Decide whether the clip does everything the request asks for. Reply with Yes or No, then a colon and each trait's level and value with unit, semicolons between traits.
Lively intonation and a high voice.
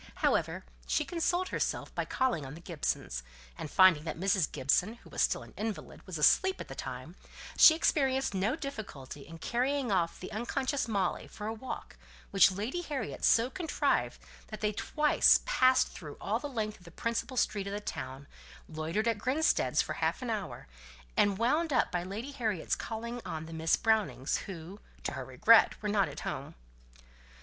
Yes: wide, 6.6 semitones; high, 215 Hz